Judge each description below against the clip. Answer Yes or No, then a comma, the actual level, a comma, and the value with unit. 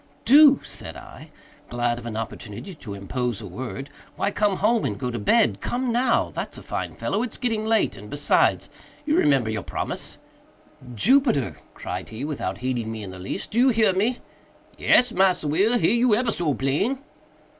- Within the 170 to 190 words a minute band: Yes, average, 180 wpm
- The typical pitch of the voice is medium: Yes, medium, 170 Hz